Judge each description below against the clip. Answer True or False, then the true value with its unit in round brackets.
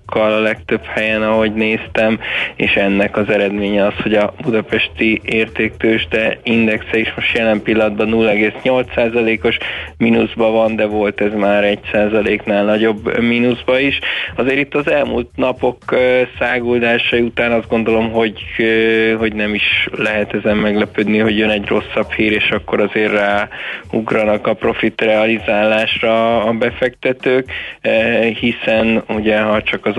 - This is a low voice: True (110 Hz)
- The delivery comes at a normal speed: True (130 wpm)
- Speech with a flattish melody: True (1.4 semitones)